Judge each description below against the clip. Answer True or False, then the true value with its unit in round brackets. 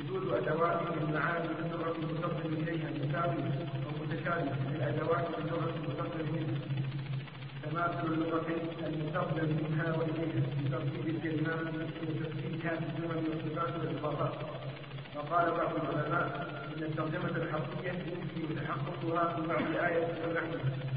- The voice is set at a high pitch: False (160 Hz)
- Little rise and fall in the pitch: True (1.6 semitones)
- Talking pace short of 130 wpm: True (115 wpm)